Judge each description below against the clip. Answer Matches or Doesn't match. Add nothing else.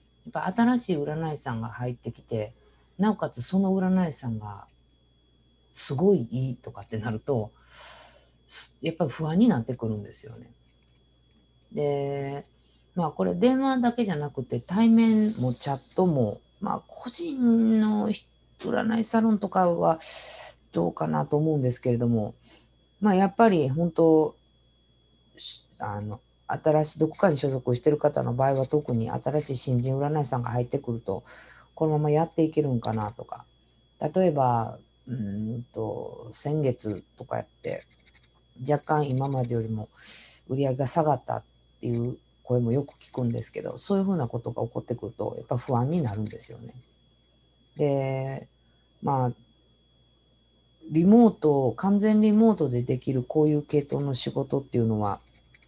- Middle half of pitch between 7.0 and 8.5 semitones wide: Doesn't match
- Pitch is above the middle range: Doesn't match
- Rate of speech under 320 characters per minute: Matches